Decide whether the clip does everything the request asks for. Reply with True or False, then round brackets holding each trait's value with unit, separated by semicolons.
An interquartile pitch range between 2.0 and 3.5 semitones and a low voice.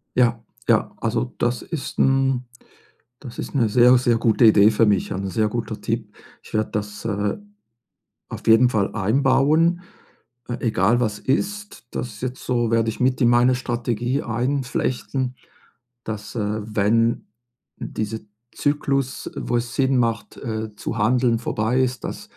True (2.7 semitones; 120 Hz)